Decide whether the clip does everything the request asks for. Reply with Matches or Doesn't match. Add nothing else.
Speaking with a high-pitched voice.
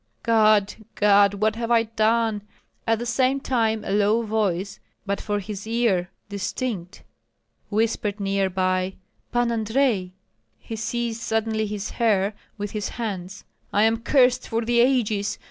Matches